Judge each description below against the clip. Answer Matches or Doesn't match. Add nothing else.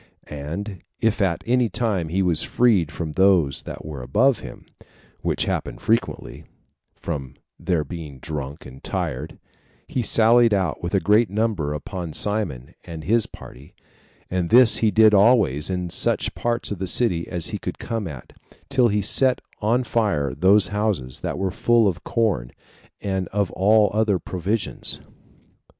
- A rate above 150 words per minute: Matches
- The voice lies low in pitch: Matches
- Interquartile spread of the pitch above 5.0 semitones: Matches